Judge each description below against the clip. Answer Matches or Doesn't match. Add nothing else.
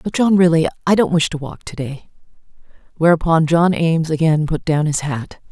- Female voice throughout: Matches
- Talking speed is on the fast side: Doesn't match